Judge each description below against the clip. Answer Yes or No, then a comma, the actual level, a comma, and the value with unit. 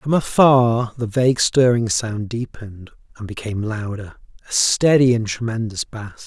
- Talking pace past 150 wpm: No, average, 145 wpm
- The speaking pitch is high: No, low, 115 Hz